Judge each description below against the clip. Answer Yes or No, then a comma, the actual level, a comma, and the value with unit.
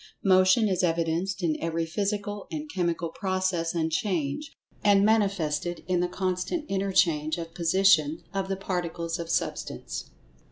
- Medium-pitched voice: Yes, medium, 180 Hz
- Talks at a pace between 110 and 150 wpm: Yes, slow, 135 wpm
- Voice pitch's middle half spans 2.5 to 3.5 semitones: Yes, average, 2.9 semitones